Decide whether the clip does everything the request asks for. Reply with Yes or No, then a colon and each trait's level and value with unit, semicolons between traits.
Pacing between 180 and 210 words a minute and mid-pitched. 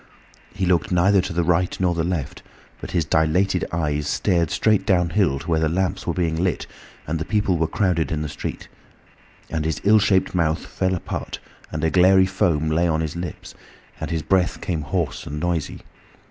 No: average, 195 wpm; very low, 85 Hz